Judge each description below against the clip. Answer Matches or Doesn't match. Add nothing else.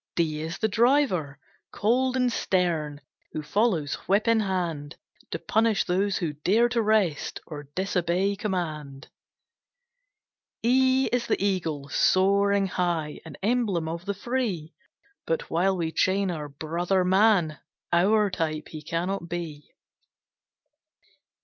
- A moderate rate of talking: Doesn't match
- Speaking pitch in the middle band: Matches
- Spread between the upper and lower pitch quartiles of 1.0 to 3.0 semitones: Doesn't match